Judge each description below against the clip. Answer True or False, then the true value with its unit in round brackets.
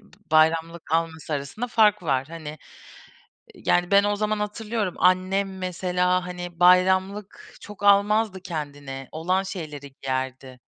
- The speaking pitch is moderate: True (180 Hz)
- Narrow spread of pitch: False (4.1 semitones)